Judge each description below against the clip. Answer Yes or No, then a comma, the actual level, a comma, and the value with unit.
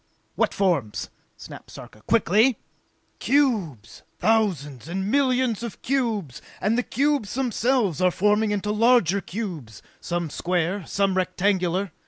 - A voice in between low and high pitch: No, high, 200 Hz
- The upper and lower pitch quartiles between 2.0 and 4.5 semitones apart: No, average, 4.9 semitones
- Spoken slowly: Yes, slow, 120 wpm